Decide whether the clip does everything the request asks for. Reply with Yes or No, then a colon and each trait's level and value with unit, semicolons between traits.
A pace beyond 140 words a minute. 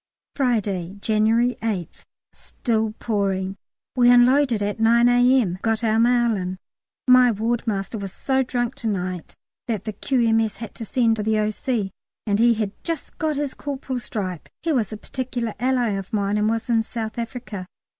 Yes: average, 165 wpm